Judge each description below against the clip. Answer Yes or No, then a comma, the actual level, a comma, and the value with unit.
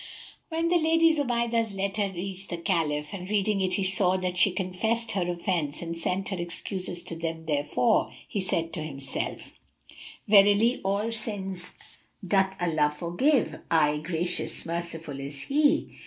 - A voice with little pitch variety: No, average, 4.1 semitones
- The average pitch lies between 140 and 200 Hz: Yes, medium, 185 Hz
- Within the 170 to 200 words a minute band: No, average, 150 wpm